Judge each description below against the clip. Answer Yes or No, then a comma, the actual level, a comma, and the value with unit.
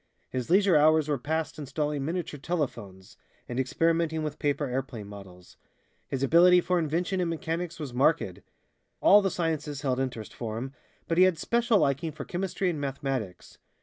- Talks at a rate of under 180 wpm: Yes, average, 165 wpm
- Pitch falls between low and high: Yes, medium, 150 Hz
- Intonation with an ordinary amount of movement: Yes, average, 4.3 semitones